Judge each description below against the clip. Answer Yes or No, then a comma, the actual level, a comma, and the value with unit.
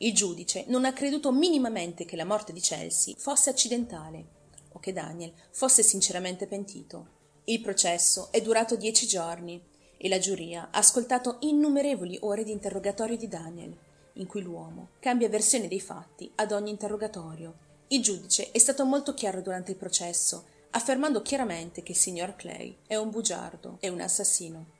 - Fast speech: No, average, 160 wpm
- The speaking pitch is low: No, high, 200 Hz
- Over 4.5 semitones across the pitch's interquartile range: Yes, average, 5.0 semitones